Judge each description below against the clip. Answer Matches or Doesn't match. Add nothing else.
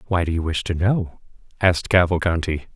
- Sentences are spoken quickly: Doesn't match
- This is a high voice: Doesn't match